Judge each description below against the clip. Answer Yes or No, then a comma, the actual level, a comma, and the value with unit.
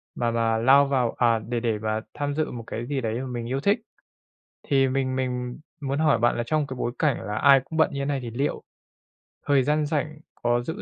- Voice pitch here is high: No, low, 130 Hz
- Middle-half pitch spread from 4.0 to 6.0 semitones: No, average, 3.2 semitones